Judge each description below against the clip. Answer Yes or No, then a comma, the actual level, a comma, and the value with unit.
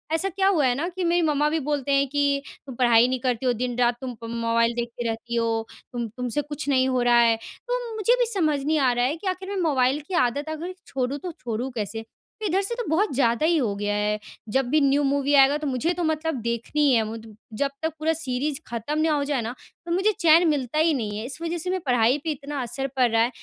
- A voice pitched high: Yes, very high, 275 Hz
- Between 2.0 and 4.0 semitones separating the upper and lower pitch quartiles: No, average, 4.8 semitones